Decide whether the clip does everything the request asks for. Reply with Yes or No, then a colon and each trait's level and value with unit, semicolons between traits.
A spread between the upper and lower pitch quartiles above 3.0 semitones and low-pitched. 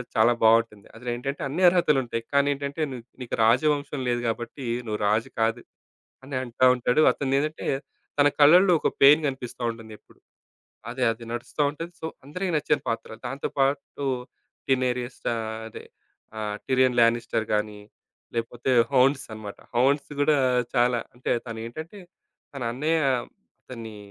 Yes: average, 3.6 semitones; low, 130 Hz